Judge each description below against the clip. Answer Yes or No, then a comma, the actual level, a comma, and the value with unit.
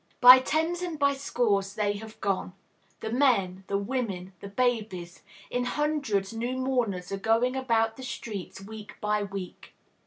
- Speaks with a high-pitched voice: Yes, high, 225 Hz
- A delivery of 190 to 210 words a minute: No, average, 155 wpm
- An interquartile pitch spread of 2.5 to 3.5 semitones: No, average, 4.4 semitones